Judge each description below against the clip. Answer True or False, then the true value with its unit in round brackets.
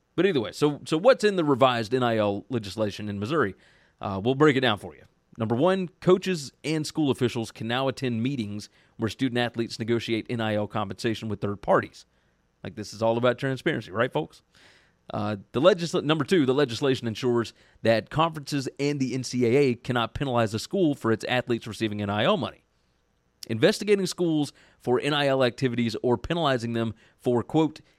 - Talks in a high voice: False (120 Hz)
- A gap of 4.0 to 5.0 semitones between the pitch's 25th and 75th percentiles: True (4.5 semitones)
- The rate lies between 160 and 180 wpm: True (170 wpm)